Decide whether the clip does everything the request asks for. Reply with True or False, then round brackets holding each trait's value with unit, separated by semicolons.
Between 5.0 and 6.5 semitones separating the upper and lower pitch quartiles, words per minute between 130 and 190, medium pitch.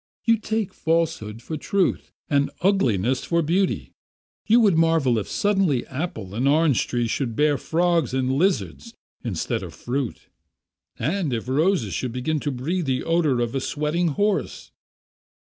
True (5.6 semitones; 150 wpm; 150 Hz)